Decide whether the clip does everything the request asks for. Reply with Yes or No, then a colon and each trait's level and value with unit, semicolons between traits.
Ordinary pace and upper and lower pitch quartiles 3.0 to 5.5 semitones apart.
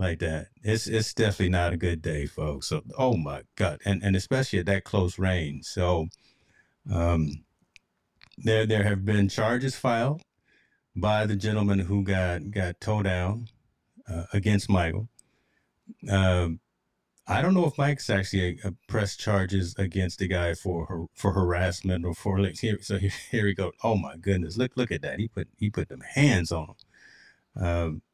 Yes: average, 175 wpm; average, 3.6 semitones